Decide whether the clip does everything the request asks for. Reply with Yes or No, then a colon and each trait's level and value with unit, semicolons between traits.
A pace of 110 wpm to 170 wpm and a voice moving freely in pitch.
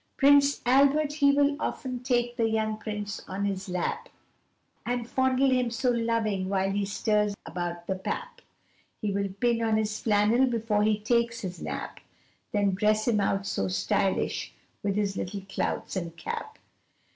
No: average, 160 wpm; average, 3.7 semitones